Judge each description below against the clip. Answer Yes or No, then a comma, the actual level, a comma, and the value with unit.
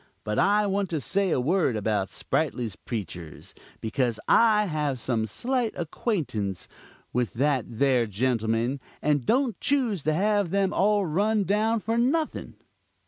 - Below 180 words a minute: Yes, average, 140 wpm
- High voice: No, medium, 155 Hz